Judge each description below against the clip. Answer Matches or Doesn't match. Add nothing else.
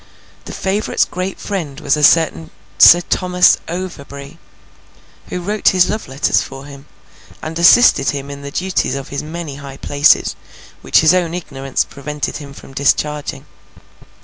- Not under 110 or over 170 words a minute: Matches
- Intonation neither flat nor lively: Matches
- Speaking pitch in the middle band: Matches